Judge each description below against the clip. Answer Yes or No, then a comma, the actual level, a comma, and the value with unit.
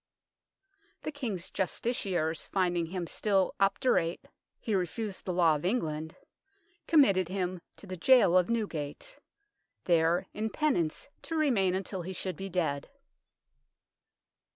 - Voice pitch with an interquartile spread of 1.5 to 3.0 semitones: No, average, 4.2 semitones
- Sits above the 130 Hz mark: Yes, medium, 185 Hz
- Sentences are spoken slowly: Yes, slow, 130 wpm